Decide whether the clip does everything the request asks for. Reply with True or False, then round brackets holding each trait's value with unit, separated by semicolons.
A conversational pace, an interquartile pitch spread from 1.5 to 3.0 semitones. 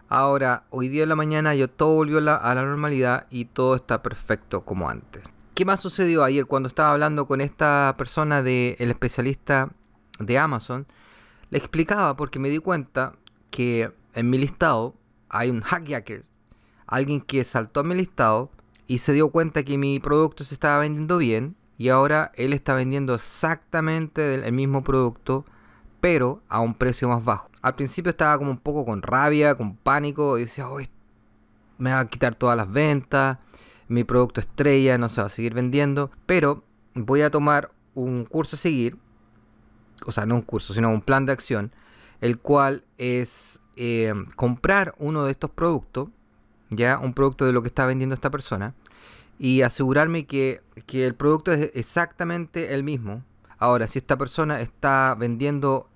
False (170 wpm; 3.6 semitones)